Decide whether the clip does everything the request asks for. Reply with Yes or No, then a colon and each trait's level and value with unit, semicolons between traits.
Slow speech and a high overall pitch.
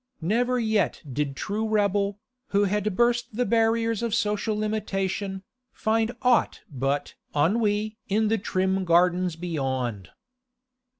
Yes: slow, 120 wpm; high, 205 Hz